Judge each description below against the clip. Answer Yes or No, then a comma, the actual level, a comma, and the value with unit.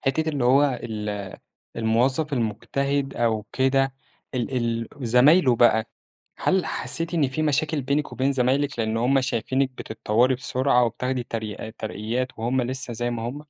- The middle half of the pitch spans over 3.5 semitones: No, average, 3.1 semitones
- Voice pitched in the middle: No, low, 125 Hz